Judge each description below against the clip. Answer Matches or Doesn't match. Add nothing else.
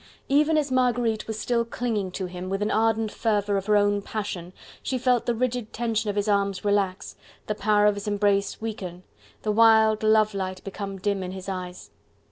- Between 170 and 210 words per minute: Matches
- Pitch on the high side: Matches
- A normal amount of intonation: Doesn't match